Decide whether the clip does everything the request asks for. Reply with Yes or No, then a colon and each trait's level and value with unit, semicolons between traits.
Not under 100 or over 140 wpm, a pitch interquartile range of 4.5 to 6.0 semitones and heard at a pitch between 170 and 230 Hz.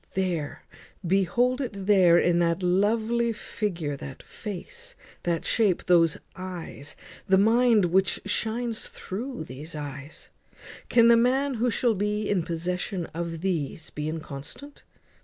Yes: slow, 135 wpm; wide, 5.5 semitones; high, 190 Hz